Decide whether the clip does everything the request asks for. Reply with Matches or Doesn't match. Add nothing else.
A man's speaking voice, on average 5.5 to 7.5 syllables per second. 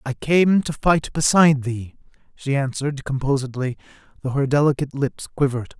Matches